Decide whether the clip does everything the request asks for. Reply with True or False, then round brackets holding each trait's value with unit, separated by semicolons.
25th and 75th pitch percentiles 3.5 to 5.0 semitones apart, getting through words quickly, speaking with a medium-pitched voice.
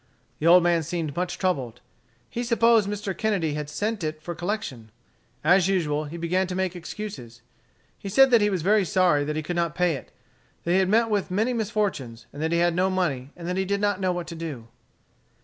True (4.3 semitones; 220 wpm; 180 Hz)